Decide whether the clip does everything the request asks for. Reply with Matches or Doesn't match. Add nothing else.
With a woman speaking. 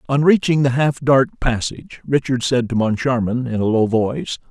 Doesn't match